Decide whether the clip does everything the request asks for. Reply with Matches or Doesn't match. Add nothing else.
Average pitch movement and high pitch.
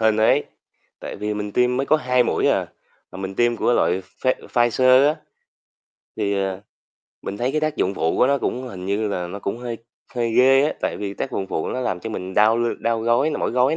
Doesn't match